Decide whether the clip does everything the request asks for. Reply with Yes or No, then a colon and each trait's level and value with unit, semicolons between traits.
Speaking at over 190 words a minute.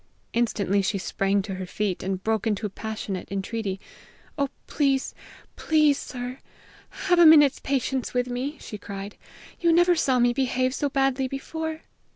No: average, 155 wpm